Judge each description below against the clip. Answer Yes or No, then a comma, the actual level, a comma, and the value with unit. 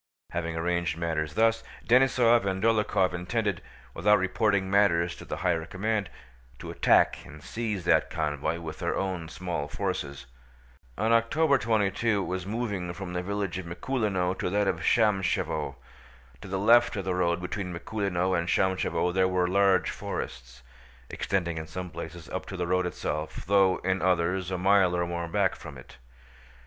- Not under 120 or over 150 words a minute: No, average, 165 wpm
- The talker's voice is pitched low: Yes, very low, 95 Hz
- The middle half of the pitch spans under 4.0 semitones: Yes, average, 2.9 semitones